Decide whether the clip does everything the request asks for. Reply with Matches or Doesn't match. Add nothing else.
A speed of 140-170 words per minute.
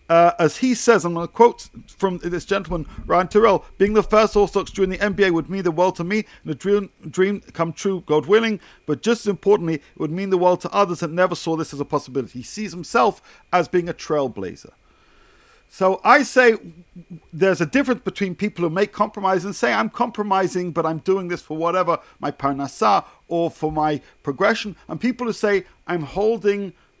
Doesn't match